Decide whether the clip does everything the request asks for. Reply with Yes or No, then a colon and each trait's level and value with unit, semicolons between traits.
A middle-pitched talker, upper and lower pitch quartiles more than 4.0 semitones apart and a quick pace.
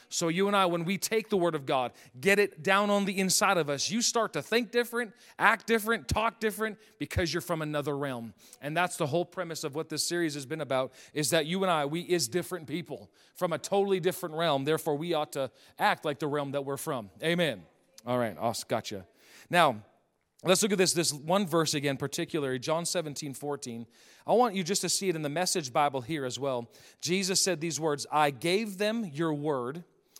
Yes: medium, 165 Hz; average, 4.7 semitones; fast, 220 wpm